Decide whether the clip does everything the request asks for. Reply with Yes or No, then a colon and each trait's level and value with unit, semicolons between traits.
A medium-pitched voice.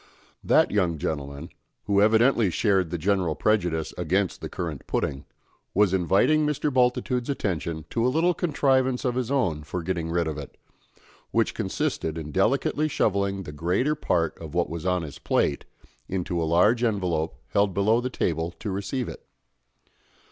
No: very low, 95 Hz